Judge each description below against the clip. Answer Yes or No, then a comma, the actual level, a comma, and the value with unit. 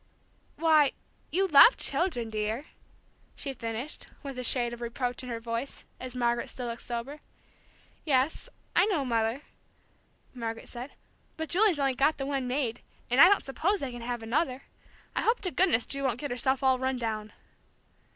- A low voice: No, very high, 255 Hz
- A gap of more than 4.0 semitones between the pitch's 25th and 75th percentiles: No, average, 3.7 semitones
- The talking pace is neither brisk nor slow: Yes, average, 170 wpm